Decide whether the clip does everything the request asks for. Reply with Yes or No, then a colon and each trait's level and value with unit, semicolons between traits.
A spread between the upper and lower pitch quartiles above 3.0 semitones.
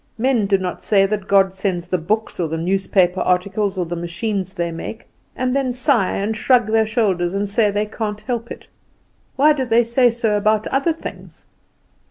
Yes: average, 3.7 semitones